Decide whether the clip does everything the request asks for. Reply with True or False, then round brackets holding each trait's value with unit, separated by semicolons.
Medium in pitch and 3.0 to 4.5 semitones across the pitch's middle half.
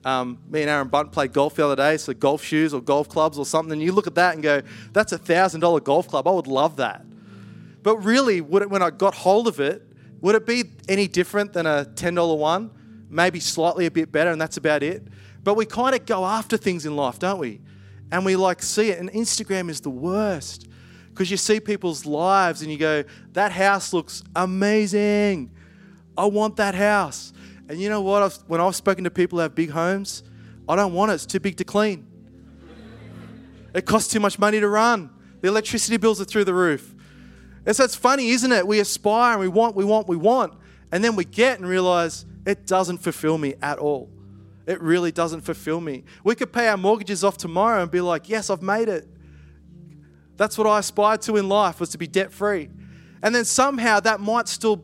False (180 Hz; 5.0 semitones)